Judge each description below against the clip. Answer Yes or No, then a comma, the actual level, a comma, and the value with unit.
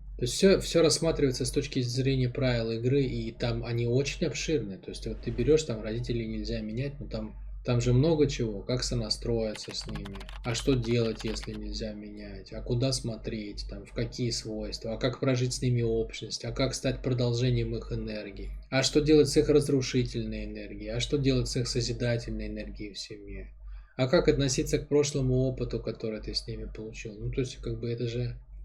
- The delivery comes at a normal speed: No, fast, 195 wpm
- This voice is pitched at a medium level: No, low, 120 Hz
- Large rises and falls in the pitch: No, average, 3.2 semitones